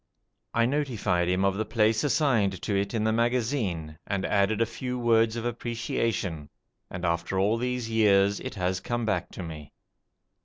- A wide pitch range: No, average, 3.8 semitones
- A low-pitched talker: Yes, low, 110 Hz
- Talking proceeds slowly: No, average, 170 wpm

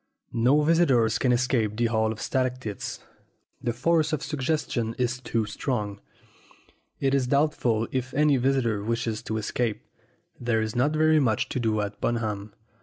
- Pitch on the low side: Yes, low, 120 Hz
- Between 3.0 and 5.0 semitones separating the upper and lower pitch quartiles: Yes, average, 3.7 semitones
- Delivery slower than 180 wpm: Yes, average, 155 wpm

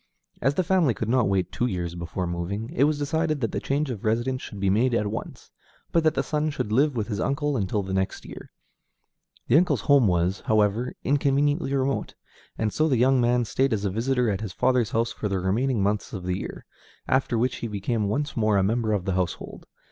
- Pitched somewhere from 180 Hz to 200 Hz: No, low, 115 Hz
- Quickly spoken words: Yes, fast, 225 wpm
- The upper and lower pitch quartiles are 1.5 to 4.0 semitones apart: No, average, 5.3 semitones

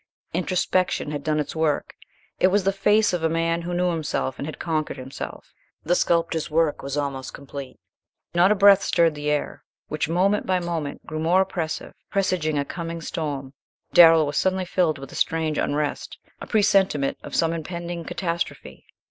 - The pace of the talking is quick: No, average, 175 wpm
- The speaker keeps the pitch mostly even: No, average, 3.2 semitones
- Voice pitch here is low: No, medium, 165 Hz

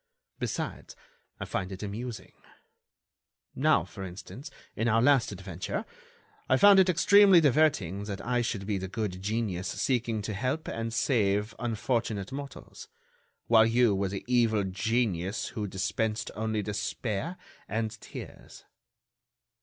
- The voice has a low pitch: Yes, low, 110 Hz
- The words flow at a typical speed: No, slow, 130 wpm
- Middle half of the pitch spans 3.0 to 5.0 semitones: Yes, average, 3.8 semitones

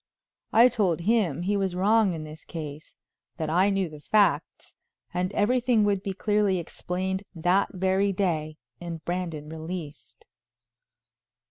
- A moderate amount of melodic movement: Yes, average, 3.7 semitones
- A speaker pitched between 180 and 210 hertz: Yes, medium, 185 Hz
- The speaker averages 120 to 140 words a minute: Yes, slow, 135 wpm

